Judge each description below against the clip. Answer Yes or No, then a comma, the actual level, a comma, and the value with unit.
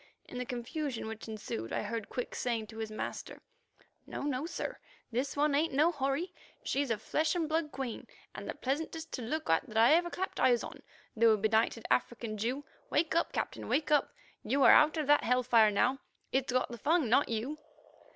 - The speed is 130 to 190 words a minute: No, average, 200 wpm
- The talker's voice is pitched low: No, very high, 260 Hz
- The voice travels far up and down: No, average, 4.9 semitones